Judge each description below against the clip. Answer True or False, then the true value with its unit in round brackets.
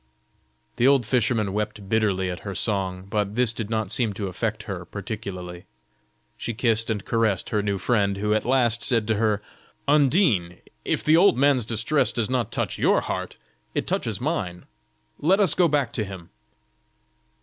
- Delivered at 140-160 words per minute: False (170 wpm)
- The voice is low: True (110 Hz)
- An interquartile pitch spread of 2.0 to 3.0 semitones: False (3.8 semitones)